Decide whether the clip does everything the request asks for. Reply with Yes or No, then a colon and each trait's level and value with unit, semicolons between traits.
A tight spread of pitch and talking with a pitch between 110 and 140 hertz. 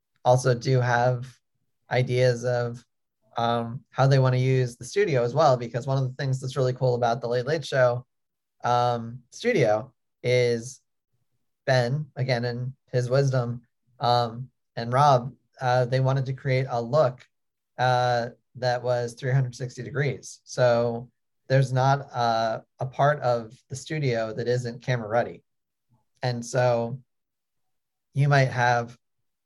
Yes: narrow, 1.4 semitones; low, 125 Hz